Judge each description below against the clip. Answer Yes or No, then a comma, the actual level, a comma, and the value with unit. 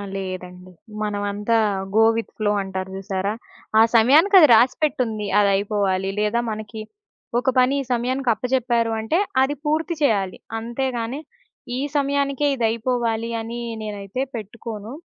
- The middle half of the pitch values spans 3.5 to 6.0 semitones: Yes, average, 4.0 semitones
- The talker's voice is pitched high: Yes, high, 225 Hz